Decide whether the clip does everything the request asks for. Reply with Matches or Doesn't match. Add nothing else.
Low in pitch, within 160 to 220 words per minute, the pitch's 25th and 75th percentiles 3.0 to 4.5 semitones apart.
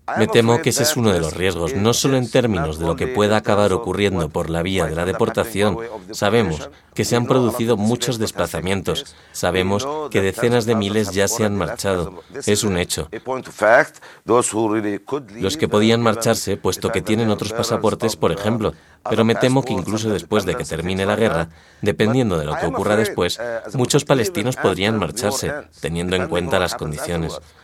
Matches